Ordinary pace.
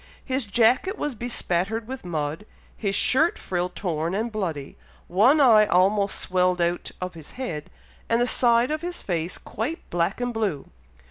Yes: average, 160 wpm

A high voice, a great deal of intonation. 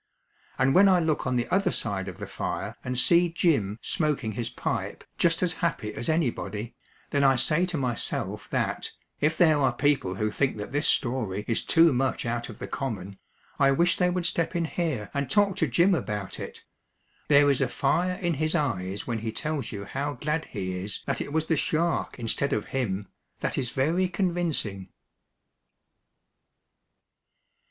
No: medium, 140 Hz; wide, 6.7 semitones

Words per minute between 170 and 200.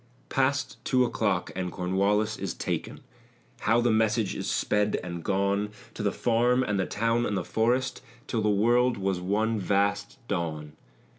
No: average, 160 wpm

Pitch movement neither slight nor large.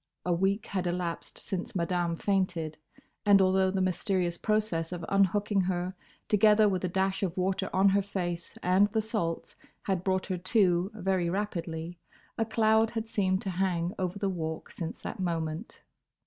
No: narrow, 2.3 semitones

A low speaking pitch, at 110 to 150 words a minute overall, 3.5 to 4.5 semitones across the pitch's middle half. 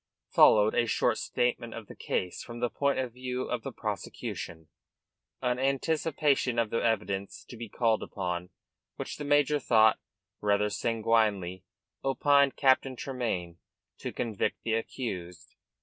Yes: low, 115 Hz; average, 140 wpm; average, 4.0 semitones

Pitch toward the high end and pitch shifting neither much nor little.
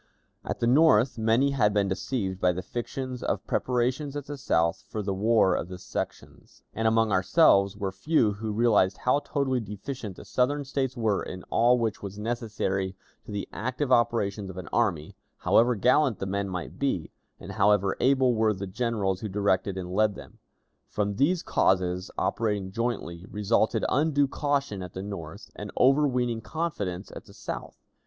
No: low, 110 Hz; average, 4.6 semitones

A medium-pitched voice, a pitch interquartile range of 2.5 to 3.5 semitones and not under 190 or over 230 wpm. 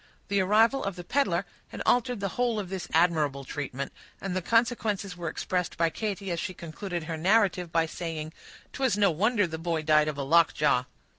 No: medium, 180 Hz; average, 4.2 semitones; average, 195 wpm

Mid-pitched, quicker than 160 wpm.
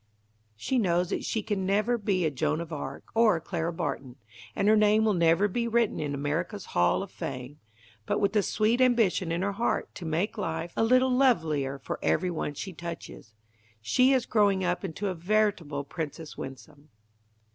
Yes: medium, 180 Hz; average, 190 wpm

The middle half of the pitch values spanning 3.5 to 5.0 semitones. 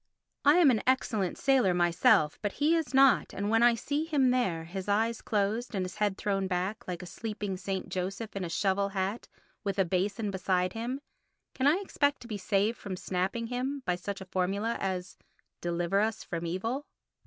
Yes: average, 4.3 semitones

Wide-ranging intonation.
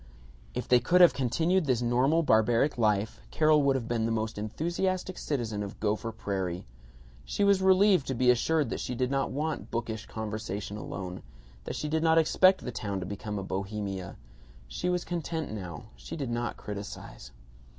Yes: wide, 7.2 semitones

